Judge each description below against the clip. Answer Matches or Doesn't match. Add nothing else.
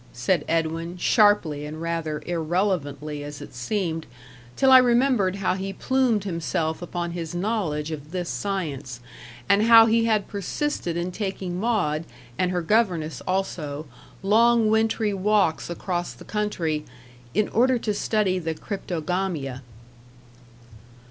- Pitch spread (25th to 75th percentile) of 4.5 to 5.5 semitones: Matches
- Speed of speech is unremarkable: Doesn't match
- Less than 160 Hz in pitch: Doesn't match